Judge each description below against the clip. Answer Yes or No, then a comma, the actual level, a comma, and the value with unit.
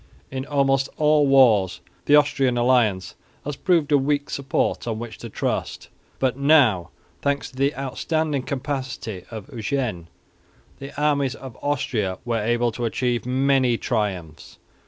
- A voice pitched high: No, low, 130 Hz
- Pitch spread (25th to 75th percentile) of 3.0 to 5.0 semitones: Yes, average, 3.4 semitones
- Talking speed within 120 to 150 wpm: Yes, average, 140 wpm